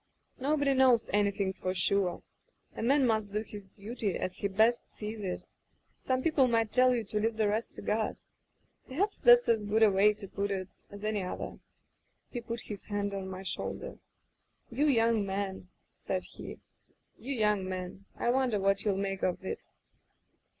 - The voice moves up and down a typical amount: Yes, average, 3.1 semitones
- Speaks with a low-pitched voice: No, high, 210 Hz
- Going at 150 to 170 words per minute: No, average, 185 wpm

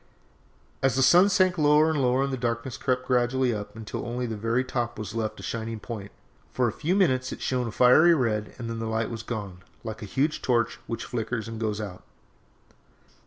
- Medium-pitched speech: No, low, 120 Hz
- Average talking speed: No, fast, 210 wpm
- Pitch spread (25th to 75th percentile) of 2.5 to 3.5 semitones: Yes, average, 2.8 semitones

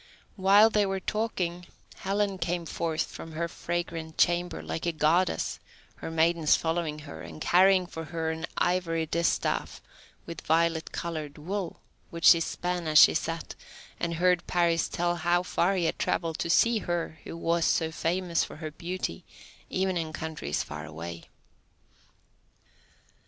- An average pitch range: No, narrow, 1.8 semitones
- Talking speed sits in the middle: Yes, average, 150 wpm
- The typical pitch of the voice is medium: Yes, medium, 170 Hz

